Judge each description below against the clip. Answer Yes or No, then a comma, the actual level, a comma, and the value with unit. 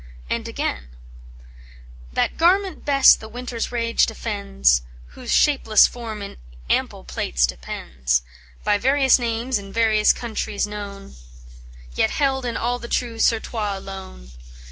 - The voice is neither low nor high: No, high, 220 Hz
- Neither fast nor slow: No, slow, 125 wpm